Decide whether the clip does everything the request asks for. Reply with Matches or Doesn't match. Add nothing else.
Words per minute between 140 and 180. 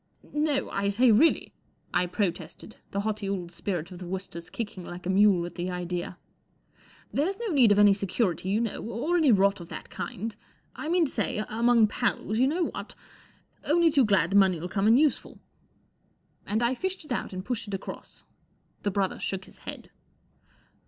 Doesn't match